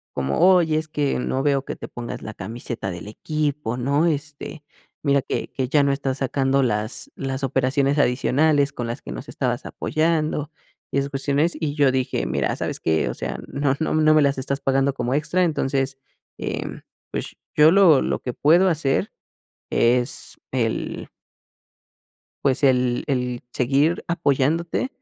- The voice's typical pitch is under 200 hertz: Yes, medium, 140 Hz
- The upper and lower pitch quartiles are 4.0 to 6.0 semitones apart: No, average, 3.1 semitones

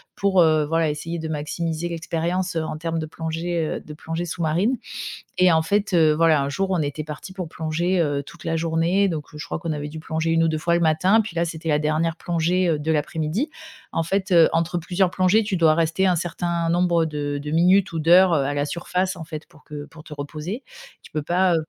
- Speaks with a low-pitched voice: No, medium, 165 Hz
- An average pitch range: No, narrow, 2.2 semitones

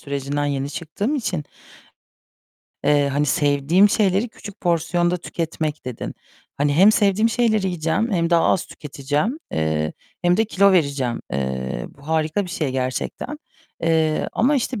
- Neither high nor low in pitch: Yes, medium, 160 Hz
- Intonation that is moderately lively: No, wide, 5.7 semitones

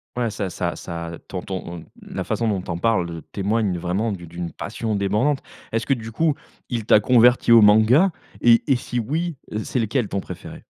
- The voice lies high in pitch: No, low, 110 Hz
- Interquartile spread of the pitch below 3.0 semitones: No, average, 4.3 semitones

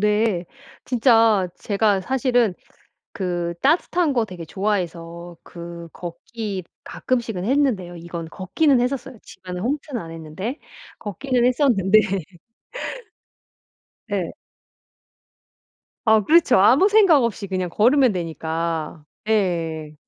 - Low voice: No, high, 205 Hz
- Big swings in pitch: Yes, wide, 6.2 semitones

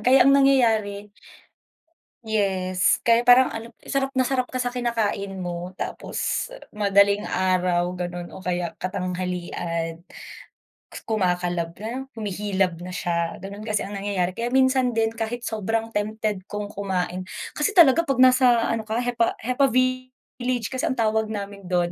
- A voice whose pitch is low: No, high, 210 Hz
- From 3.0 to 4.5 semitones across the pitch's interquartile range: No, average, 4.9 semitones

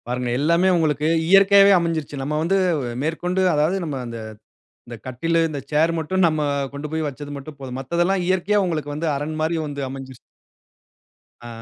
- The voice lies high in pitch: No, medium, 155 Hz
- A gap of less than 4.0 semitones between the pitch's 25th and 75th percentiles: Yes, average, 3.3 semitones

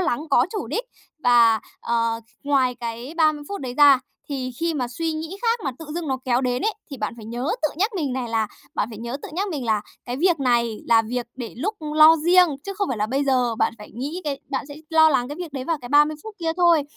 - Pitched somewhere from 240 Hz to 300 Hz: Yes, very high, 275 Hz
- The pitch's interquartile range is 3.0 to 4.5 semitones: No, average, 5.1 semitones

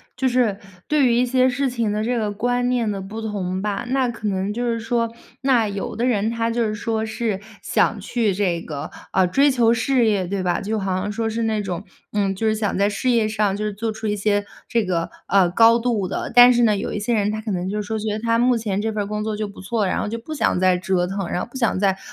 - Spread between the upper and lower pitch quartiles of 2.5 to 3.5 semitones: Yes, average, 2.8 semitones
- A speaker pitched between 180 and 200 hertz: No, high, 215 Hz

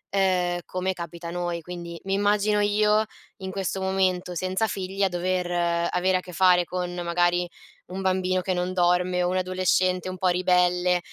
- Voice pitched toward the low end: No, medium, 185 Hz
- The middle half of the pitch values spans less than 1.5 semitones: Yes, narrow, 1.0 semitones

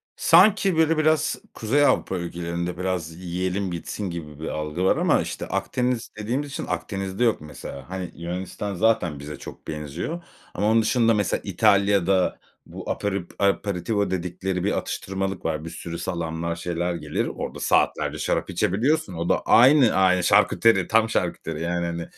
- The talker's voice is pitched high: No, very low, 95 Hz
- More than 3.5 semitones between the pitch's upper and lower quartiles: Yes, average, 4.4 semitones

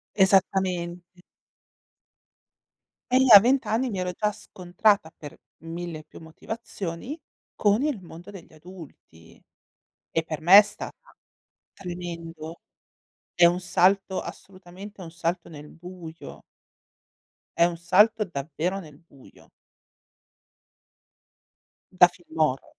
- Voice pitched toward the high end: No, medium, 180 Hz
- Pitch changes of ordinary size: Yes, average, 3.0 semitones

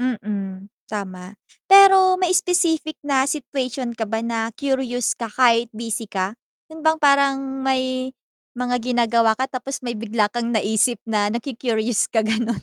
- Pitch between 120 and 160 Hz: No, high, 240 Hz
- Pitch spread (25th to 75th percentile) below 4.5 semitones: Yes, average, 3.4 semitones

